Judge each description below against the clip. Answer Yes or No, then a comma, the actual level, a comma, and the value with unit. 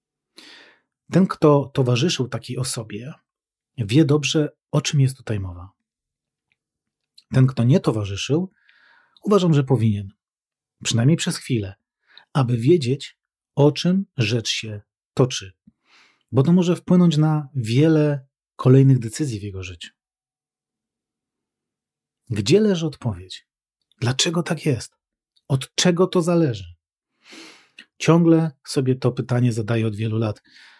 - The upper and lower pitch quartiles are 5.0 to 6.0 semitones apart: Yes, wide, 5.5 semitones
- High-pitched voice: No, low, 135 Hz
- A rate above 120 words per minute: No, average, 115 wpm